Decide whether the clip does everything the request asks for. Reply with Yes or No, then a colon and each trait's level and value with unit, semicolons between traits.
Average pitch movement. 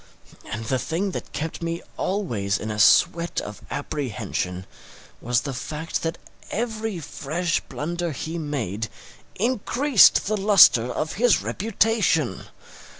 No: wide, 8.2 semitones